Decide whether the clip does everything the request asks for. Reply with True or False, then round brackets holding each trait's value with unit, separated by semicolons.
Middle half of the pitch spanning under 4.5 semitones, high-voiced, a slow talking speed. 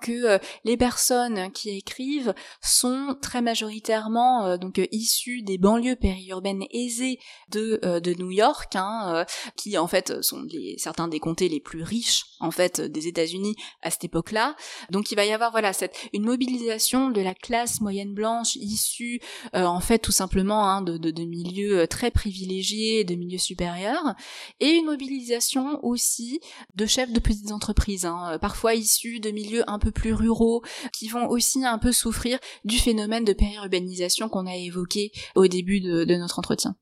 False (4.1 semitones; 215 Hz; 175 wpm)